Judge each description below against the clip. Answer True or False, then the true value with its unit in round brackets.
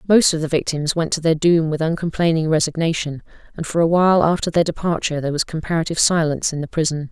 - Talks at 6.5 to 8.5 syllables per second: True (6.8 syllables/s)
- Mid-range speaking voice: True (160 Hz)